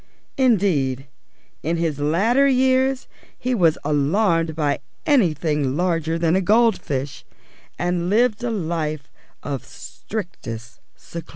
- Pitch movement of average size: No, wide, 6.7 semitones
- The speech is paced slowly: Yes, slow, 110 wpm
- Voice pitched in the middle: Yes, medium, 170 Hz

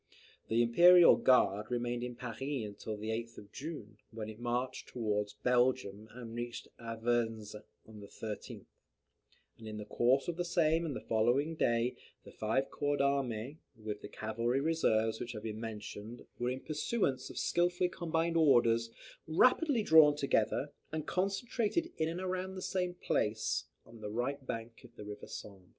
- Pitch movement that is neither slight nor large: No, wide, 6.0 semitones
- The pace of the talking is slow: No, average, 165 wpm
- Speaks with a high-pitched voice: No, low, 120 Hz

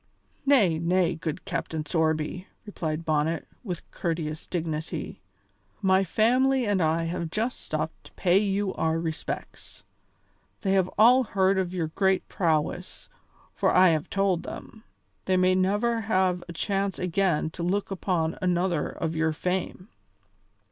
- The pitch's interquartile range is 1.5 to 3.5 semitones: Yes, average, 3.2 semitones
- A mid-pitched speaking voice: Yes, medium, 180 Hz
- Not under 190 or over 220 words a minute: No, average, 140 wpm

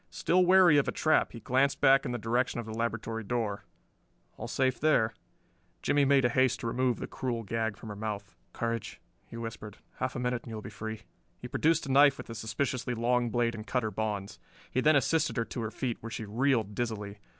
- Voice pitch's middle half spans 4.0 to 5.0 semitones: No, average, 3.0 semitones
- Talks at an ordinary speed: No, fast, 220 wpm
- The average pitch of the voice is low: Yes, low, 115 Hz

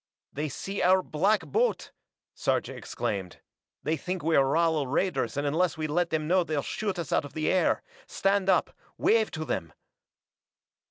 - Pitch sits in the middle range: Yes, medium, 165 Hz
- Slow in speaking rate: No, average, 165 wpm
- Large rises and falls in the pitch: No, average, 4.0 semitones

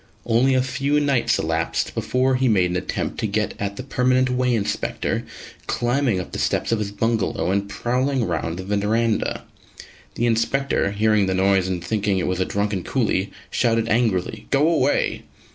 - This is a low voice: Yes, low, 110 Hz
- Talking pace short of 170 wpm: No, average, 175 wpm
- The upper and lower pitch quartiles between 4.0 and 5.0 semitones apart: Yes, average, 4.4 semitones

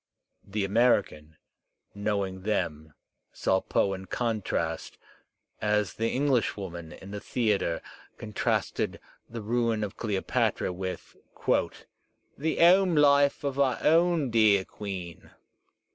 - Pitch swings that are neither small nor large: Yes, average, 4.7 semitones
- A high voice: No, low, 105 Hz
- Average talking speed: No, slow, 110 wpm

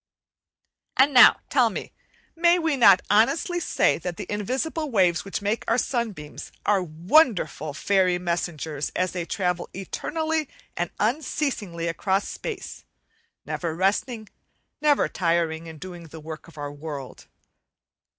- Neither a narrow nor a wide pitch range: No, wide, 7.0 semitones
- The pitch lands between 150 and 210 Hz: Yes, medium, 185 Hz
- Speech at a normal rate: No, slow, 130 wpm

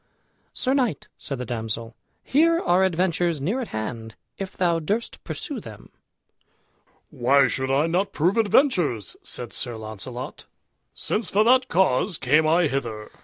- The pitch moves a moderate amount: No, wide, 8.2 semitones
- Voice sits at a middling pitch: Yes, medium, 160 Hz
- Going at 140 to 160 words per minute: Yes, average, 145 wpm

